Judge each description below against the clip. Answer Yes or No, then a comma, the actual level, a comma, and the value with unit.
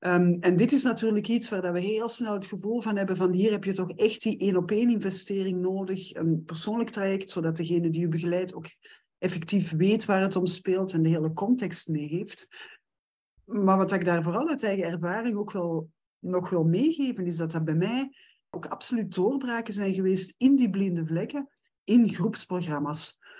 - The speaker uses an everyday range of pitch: Yes, average, 3.8 semitones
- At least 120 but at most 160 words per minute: No, average, 195 wpm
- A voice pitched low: No, high, 190 Hz